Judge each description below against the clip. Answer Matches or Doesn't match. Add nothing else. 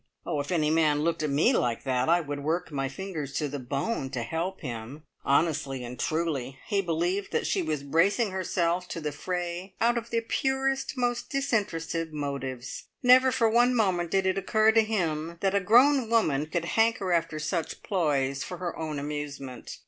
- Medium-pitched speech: Matches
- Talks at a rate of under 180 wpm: Doesn't match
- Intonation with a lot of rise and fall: Matches